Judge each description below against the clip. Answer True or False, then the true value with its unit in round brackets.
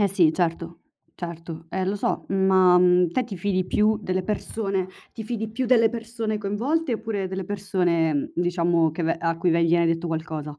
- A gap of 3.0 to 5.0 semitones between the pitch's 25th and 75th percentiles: True (3.7 semitones)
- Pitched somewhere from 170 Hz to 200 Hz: True (185 Hz)